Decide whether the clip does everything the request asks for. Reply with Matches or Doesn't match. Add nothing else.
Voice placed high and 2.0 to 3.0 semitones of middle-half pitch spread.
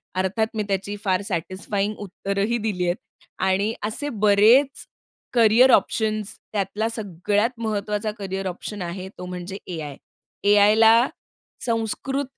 Matches